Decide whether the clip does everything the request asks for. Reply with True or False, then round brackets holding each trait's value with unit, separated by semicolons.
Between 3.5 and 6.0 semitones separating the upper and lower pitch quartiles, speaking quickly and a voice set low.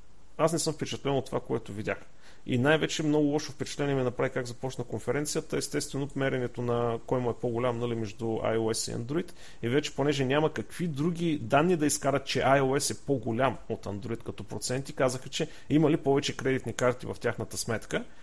True (4.0 semitones; 190 wpm; 130 Hz)